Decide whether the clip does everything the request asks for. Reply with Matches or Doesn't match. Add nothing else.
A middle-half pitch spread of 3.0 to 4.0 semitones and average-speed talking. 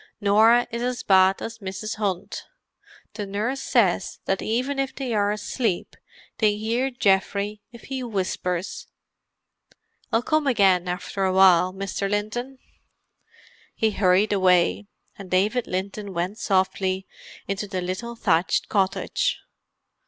Doesn't match